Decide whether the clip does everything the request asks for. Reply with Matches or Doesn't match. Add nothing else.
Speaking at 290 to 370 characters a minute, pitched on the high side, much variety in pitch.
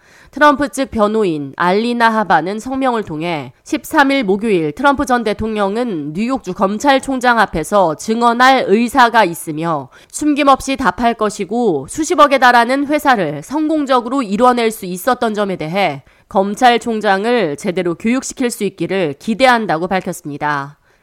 Matches